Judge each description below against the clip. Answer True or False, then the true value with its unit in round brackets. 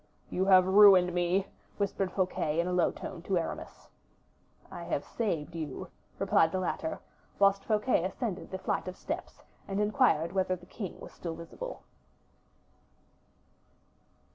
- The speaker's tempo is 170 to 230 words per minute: False (140 wpm)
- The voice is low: False (185 Hz)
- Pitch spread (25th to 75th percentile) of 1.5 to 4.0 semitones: True (2.5 semitones)